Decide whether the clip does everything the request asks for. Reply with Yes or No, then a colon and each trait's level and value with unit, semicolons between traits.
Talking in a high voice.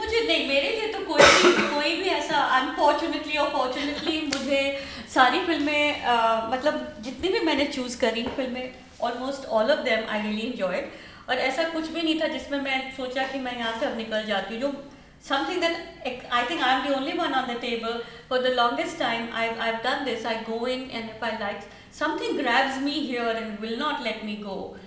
Yes: very high, 265 Hz